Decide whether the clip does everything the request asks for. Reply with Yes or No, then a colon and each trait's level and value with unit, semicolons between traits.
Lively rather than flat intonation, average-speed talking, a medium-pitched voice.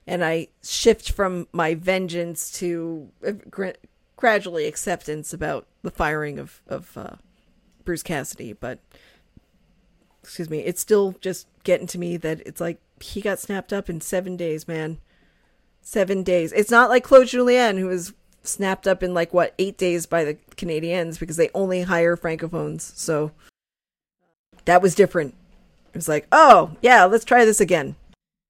No: average, 3.0 semitones; average, 155 wpm; medium, 180 Hz